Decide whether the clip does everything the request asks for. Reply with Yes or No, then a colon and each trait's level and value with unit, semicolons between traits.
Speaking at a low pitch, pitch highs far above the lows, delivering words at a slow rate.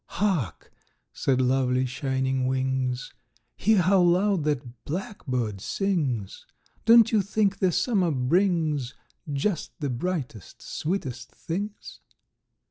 No: medium, 150 Hz; wide, 7.0 semitones; slow, 105 wpm